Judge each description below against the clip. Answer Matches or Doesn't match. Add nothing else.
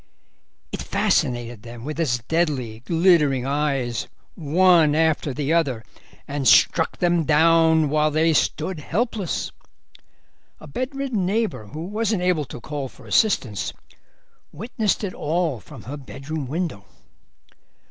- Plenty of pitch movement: Doesn't match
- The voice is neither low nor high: Matches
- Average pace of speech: Doesn't match